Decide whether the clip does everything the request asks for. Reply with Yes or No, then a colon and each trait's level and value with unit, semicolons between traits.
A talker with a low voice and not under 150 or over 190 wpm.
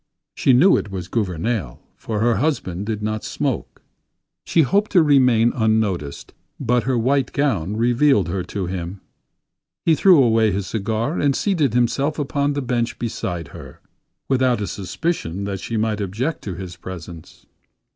Yes: low, 115 Hz; average, 155 wpm